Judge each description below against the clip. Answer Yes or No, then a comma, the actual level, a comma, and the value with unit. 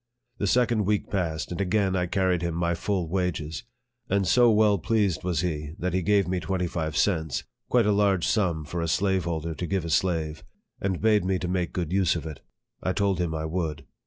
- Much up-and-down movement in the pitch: No, average, 3.1 semitones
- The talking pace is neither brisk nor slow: No, fast, 220 wpm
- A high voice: No, very low, 90 Hz